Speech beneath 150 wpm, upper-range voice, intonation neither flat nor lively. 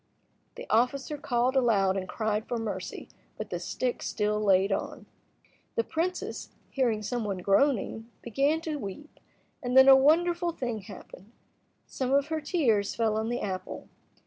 No: average, 155 wpm; high, 240 Hz; average, 4.8 semitones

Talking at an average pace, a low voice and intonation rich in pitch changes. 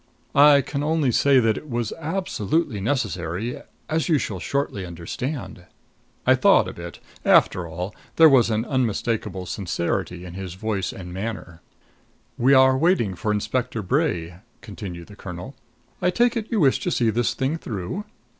Yes: average, 160 wpm; low, 115 Hz; wide, 7.3 semitones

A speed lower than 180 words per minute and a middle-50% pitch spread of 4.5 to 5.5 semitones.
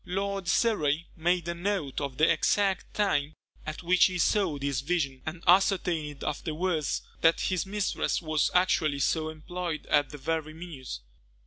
No: average, 150 wpm; average, 3.4 semitones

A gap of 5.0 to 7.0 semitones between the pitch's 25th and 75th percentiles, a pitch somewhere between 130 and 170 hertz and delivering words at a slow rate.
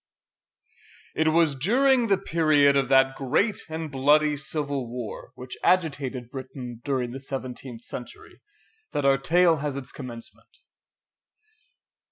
No: average, 3.5 semitones; medium, 140 Hz; slow, 125 wpm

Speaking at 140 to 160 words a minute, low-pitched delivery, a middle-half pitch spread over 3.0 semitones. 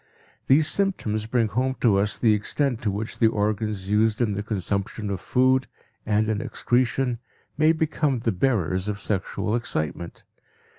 Yes: average, 155 wpm; low, 110 Hz; average, 3.7 semitones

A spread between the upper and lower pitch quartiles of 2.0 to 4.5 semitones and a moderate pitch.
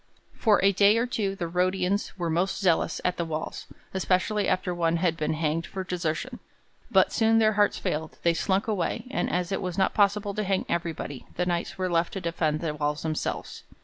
Yes: average, 3.2 semitones; medium, 180 Hz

